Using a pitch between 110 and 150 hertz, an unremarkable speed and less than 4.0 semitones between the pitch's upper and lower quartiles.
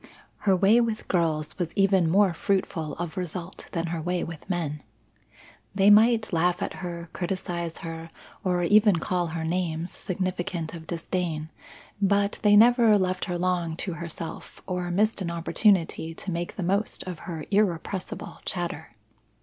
No: medium, 180 Hz; average, 155 wpm; average, 2.7 semitones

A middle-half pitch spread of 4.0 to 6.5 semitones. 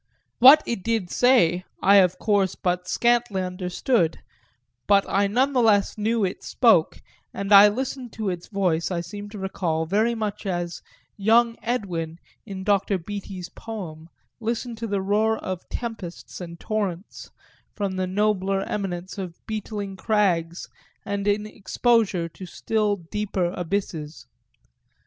No: average, 3.3 semitones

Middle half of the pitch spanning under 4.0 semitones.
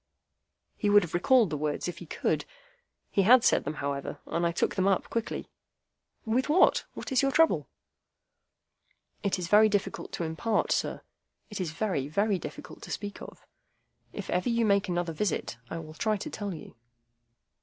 No: average, 4.6 semitones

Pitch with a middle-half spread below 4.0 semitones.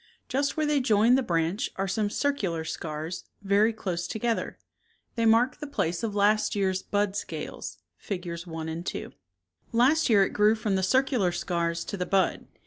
No: average, 4.6 semitones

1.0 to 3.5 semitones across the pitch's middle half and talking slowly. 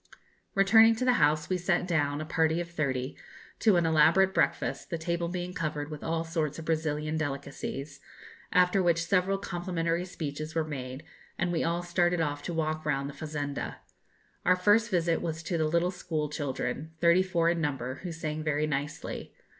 No: narrow, 2.6 semitones; average, 180 wpm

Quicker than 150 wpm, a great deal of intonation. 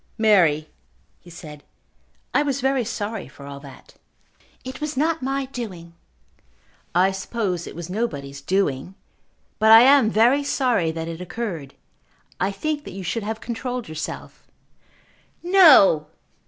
No: average, 140 wpm; wide, 7.4 semitones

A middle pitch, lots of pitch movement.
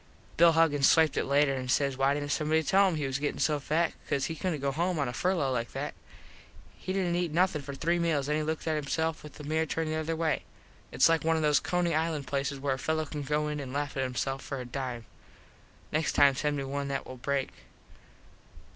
No: medium, 150 Hz; average, 2.7 semitones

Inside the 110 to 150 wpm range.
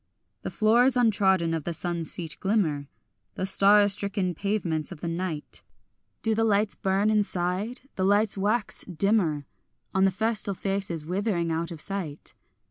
Yes: average, 145 wpm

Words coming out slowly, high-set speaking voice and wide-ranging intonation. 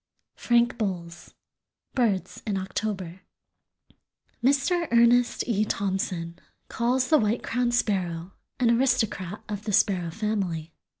No: slow, 110 wpm; high, 210 Hz; average, 4.3 semitones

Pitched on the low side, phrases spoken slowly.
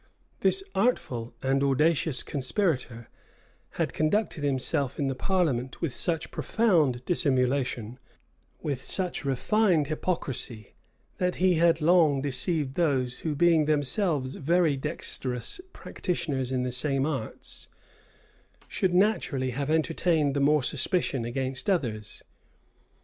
No: medium, 145 Hz; slow, 115 wpm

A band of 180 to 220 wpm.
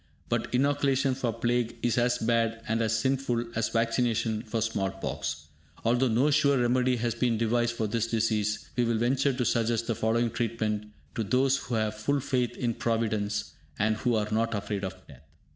Yes: average, 185 wpm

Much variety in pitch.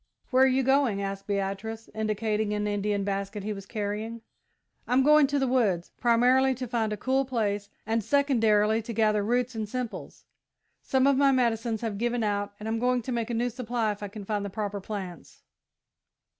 No: average, 3.3 semitones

